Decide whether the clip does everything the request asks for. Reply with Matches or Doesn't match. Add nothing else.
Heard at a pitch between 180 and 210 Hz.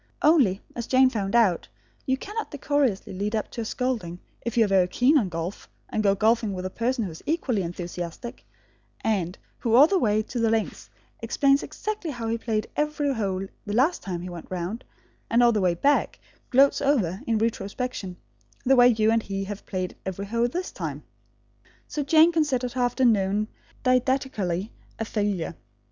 Doesn't match